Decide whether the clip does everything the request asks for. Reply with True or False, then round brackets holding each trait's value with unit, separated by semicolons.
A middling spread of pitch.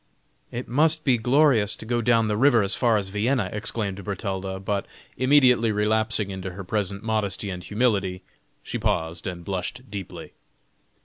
True (3.6 semitones)